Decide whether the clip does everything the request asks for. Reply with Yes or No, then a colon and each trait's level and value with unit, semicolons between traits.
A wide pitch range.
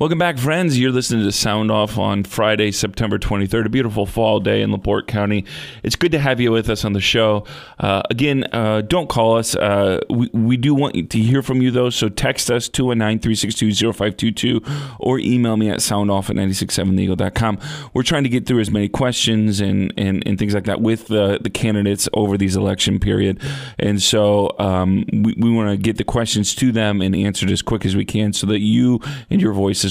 No: average, 3.3 semitones